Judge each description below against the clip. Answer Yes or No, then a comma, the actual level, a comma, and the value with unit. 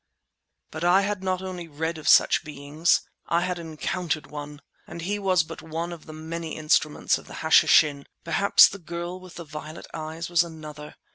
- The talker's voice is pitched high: No, medium, 165 Hz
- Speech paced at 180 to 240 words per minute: Yes, average, 185 wpm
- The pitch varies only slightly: Yes, narrow, 2.2 semitones